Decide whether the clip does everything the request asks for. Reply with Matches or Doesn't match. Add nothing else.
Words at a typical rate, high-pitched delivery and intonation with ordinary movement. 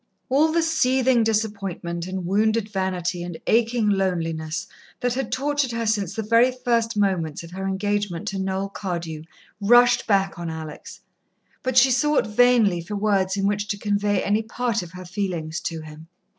Matches